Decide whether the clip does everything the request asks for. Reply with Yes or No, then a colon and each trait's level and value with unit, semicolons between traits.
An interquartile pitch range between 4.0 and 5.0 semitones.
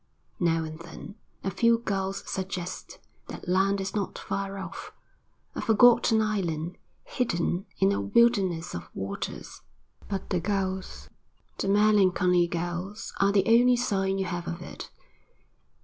No: average, 2.9 semitones